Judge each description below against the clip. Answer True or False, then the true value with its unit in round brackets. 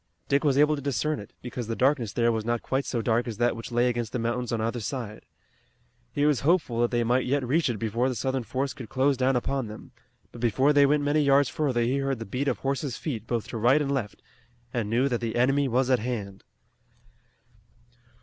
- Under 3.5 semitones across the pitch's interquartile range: True (2.9 semitones)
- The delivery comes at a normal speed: False (230 wpm)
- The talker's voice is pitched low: True (125 Hz)